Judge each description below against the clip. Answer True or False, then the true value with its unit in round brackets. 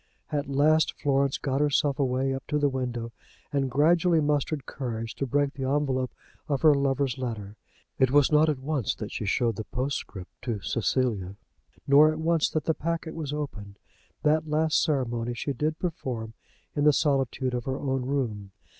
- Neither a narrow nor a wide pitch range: True (3.3 semitones)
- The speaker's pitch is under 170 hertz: True (135 Hz)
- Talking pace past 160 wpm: True (175 wpm)